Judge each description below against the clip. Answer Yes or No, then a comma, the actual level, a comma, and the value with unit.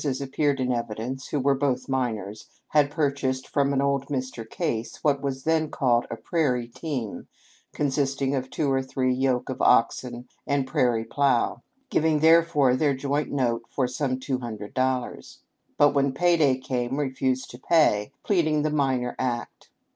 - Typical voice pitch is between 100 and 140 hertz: Yes, low, 135 Hz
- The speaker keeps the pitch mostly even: Yes, narrow, 2.2 semitones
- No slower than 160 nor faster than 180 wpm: Yes, average, 170 wpm